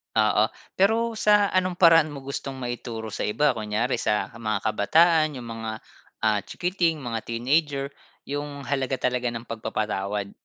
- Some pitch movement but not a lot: No, wide, 6.0 semitones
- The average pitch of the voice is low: Yes, low, 130 Hz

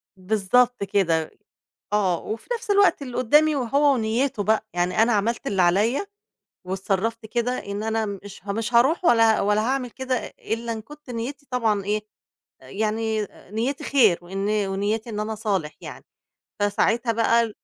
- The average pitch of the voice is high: Yes, high, 220 Hz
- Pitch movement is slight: No, average, 3.3 semitones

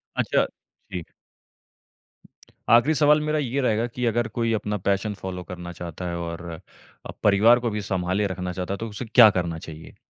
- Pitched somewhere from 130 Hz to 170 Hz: No, low, 105 Hz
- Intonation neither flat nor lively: Yes, average, 4.8 semitones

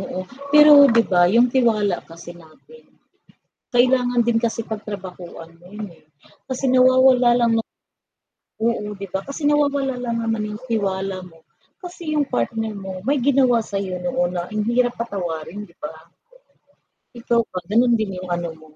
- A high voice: Yes, high, 225 Hz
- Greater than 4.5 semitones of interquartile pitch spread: Yes, average, 5.2 semitones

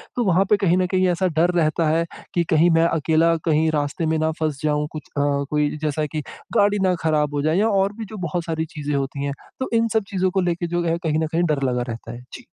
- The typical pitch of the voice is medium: Yes, medium, 165 Hz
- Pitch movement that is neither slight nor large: Yes, average, 3.2 semitones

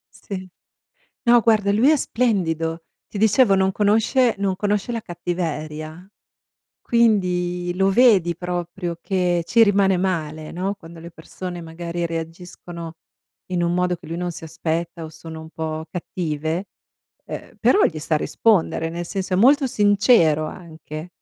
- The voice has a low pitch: No, medium, 175 Hz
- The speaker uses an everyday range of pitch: Yes, average, 3.5 semitones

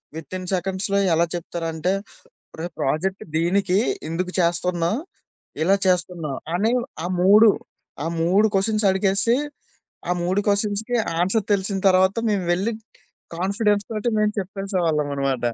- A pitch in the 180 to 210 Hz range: Yes, high, 190 Hz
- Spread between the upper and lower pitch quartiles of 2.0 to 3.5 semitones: Yes, average, 2.9 semitones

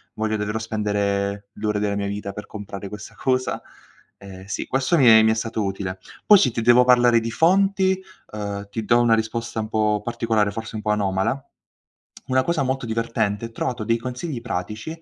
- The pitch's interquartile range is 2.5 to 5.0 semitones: Yes, average, 2.9 semitones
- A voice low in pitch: Yes, low, 110 Hz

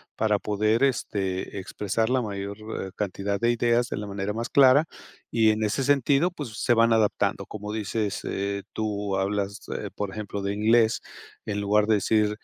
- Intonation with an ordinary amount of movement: No, narrow, 2.3 semitones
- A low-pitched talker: Yes, low, 105 Hz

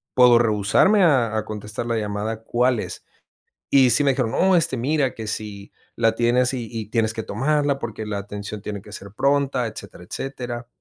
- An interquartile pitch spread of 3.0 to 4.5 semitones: Yes, average, 3.5 semitones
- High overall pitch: No, low, 115 Hz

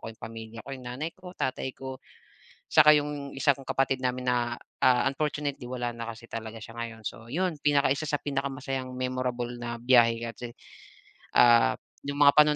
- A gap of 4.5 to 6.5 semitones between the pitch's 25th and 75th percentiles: No, average, 3.2 semitones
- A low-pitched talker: Yes, low, 130 Hz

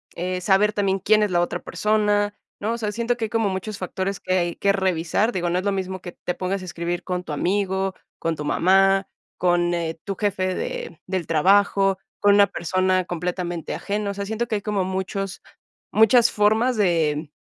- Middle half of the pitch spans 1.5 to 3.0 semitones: Yes, narrow, 2.6 semitones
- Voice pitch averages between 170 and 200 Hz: Yes, high, 190 Hz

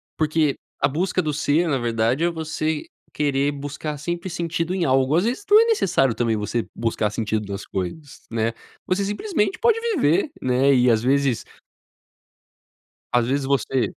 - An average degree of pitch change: No, wide, 5.9 semitones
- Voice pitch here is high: No, medium, 145 Hz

